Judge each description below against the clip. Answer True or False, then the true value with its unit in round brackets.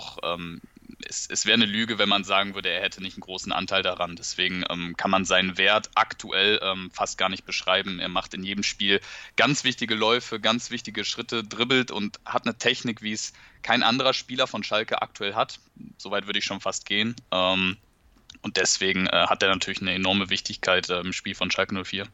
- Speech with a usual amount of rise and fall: True (3.3 semitones)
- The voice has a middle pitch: False (100 Hz)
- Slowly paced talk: False (185 wpm)